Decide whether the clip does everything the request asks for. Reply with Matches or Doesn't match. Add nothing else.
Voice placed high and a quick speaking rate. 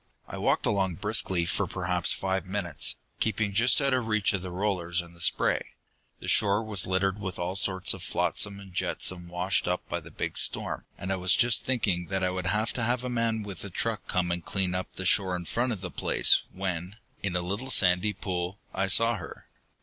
Doesn't match